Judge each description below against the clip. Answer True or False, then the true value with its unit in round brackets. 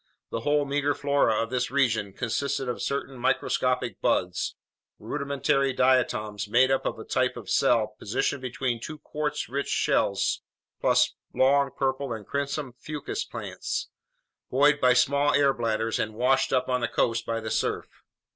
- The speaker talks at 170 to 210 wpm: False (155 wpm)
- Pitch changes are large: False (3.5 semitones)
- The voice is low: True (130 Hz)